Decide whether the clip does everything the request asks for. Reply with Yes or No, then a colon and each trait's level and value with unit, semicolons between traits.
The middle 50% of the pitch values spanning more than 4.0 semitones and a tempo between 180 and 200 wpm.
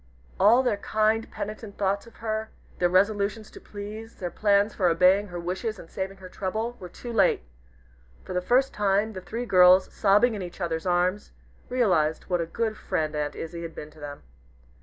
No: average, 3.5 semitones; average, 190 wpm